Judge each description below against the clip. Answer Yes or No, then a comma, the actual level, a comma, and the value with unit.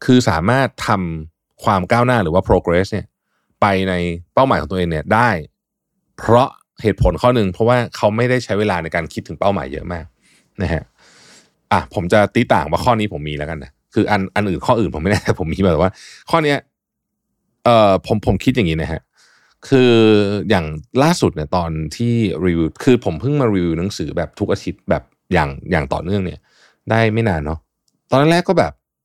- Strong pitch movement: Yes, wide, 5.8 semitones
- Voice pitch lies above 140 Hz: No, low, 100 Hz